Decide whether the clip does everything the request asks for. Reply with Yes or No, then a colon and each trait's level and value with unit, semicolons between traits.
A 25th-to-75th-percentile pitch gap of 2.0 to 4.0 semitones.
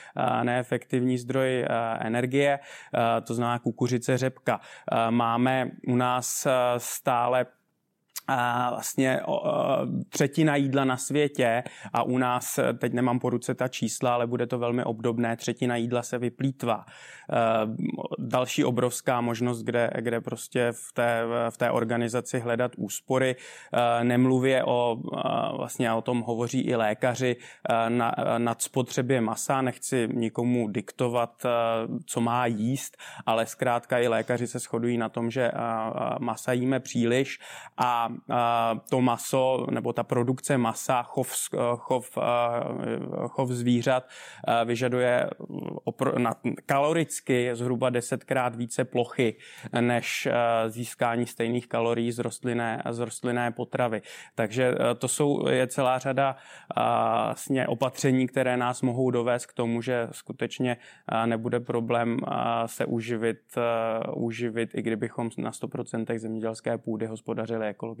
No: narrow, 1.4 semitones